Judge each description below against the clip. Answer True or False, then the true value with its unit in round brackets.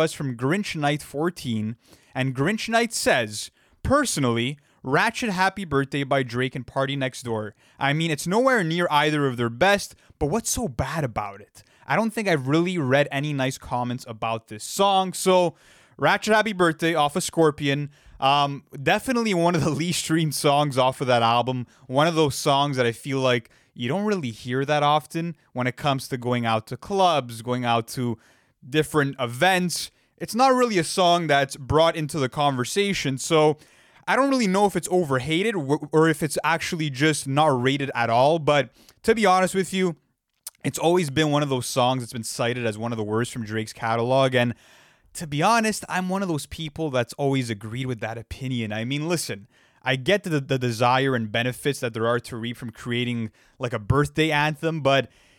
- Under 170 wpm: False (195 wpm)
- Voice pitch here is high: False (140 Hz)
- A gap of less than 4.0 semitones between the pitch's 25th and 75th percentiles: False (5.1 semitones)